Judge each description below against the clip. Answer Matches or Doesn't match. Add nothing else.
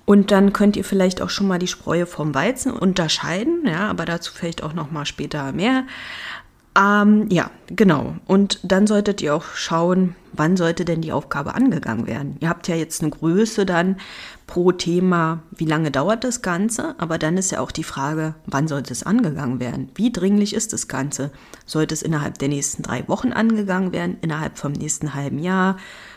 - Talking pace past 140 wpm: Matches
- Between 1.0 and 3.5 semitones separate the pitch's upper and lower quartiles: Doesn't match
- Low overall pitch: Doesn't match